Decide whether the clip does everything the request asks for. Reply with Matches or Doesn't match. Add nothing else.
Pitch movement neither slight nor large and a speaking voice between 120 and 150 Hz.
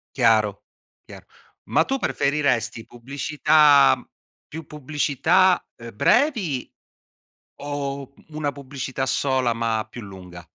Matches